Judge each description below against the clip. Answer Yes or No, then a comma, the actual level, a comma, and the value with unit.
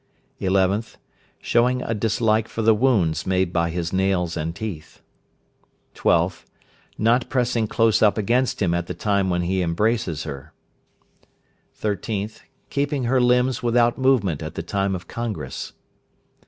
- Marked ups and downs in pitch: No, average, 5.0 semitones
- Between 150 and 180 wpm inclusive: No, average, 140 wpm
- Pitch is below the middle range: Yes, low, 105 Hz